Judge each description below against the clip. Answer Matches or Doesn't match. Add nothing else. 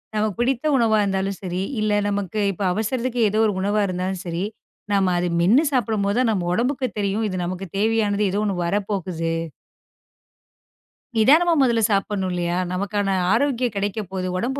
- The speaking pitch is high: Matches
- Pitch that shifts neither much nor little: Matches